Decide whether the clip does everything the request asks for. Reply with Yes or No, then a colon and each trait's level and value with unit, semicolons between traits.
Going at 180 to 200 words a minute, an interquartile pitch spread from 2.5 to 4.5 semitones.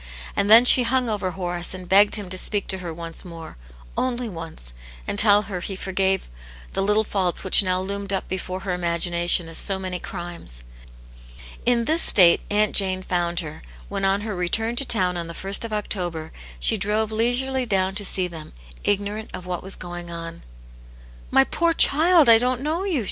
Yes: average, 190 wpm; average, 3.7 semitones